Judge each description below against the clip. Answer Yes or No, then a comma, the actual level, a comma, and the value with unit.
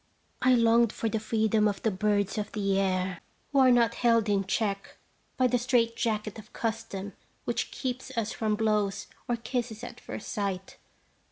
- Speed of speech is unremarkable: Yes, average, 175 wpm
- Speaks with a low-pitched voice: No, high, 220 Hz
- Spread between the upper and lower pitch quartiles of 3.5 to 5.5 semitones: No, narrow, 2.5 semitones